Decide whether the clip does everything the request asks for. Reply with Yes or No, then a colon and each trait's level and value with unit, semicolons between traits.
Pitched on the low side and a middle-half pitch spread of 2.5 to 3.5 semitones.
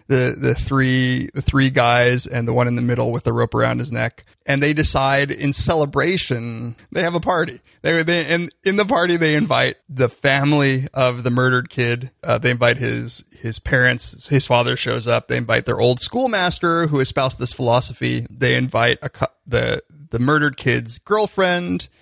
No: low, 130 Hz; average, 3.9 semitones